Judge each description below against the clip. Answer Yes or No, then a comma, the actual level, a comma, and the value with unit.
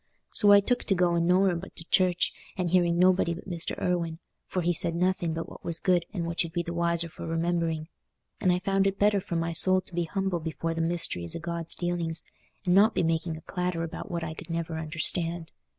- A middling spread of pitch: No, narrow, 1.6 semitones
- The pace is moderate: No, fast, 230 wpm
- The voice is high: No, medium, 170 Hz